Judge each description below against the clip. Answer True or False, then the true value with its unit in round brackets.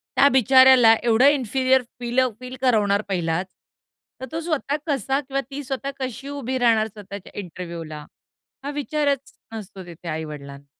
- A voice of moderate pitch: False (245 Hz)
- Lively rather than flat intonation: True (5.9 semitones)